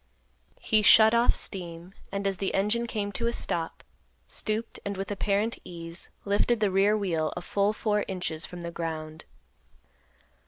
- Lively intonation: No, average, 3.7 semitones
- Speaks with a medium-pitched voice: No, high, 200 Hz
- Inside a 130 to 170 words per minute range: Yes, average, 160 wpm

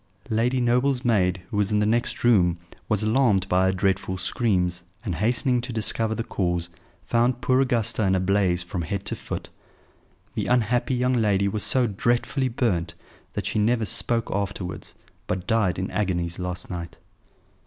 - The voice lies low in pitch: Yes, low, 105 Hz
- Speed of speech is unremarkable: Yes, average, 170 wpm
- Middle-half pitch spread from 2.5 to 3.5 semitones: No, average, 4.5 semitones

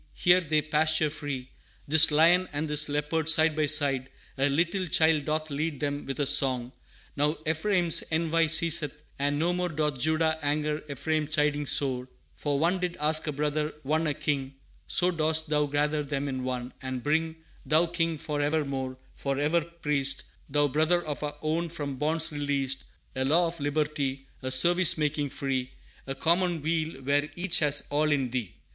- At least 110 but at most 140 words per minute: No, average, 170 wpm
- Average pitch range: No, narrow, 2.1 semitones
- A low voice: No, medium, 150 Hz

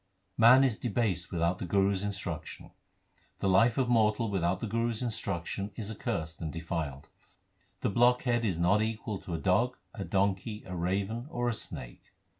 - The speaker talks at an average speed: Yes, average, 175 wpm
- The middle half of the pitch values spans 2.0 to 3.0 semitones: No, average, 4.4 semitones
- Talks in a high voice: No, low, 100 Hz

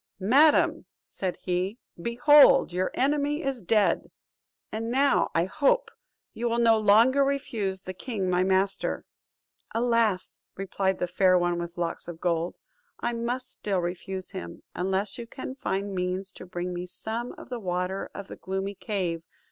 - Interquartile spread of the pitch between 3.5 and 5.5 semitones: Yes, average, 4.6 semitones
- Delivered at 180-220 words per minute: No, average, 155 wpm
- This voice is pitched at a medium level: No, high, 195 Hz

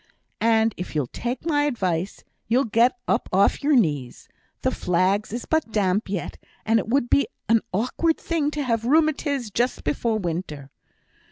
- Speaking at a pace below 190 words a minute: Yes, average, 165 wpm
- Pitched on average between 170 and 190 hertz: No, high, 225 Hz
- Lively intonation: Yes, wide, 6.2 semitones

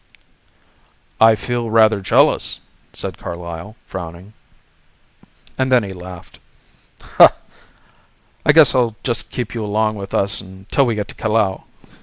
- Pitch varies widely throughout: No, average, 3.3 semitones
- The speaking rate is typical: No, slow, 125 wpm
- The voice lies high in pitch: No, low, 105 Hz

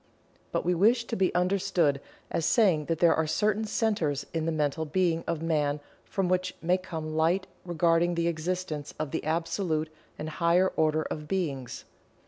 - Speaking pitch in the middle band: Yes, medium, 165 Hz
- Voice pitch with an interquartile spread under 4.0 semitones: Yes, average, 2.8 semitones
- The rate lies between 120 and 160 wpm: No, average, 170 wpm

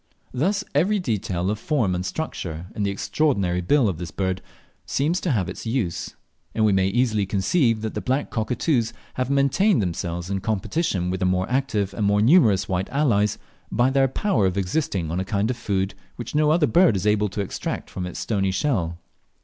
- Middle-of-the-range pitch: No, low, 105 Hz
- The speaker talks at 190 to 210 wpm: Yes, average, 200 wpm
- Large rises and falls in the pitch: Yes, wide, 6.4 semitones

